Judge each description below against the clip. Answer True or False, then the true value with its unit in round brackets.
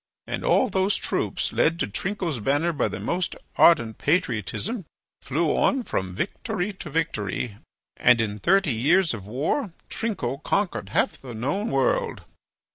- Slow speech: False (145 wpm)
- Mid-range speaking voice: True (165 Hz)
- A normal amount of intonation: False (8.4 semitones)